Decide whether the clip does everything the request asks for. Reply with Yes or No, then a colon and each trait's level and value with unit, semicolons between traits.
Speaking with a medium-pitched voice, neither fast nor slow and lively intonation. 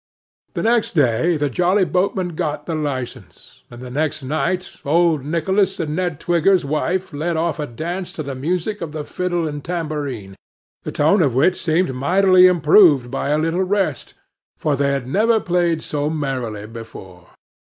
No: medium, 160 Hz; average, 170 wpm; average, 4.2 semitones